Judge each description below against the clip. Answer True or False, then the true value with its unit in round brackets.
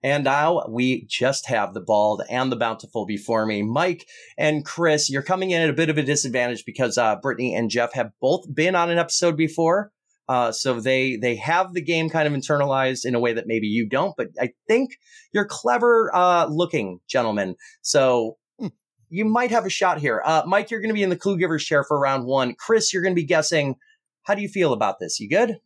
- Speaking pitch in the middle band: True (150 Hz)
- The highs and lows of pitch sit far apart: True (6.7 semitones)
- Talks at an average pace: False (225 wpm)